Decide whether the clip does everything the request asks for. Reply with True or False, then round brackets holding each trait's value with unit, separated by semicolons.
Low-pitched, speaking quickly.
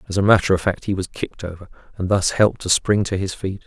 True (95 Hz; 280 wpm)